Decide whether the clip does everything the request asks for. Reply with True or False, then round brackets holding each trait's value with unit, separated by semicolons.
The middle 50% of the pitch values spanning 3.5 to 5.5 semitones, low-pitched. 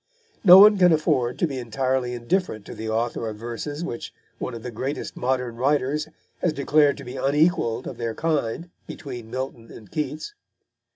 True (4.4 semitones; 130 Hz)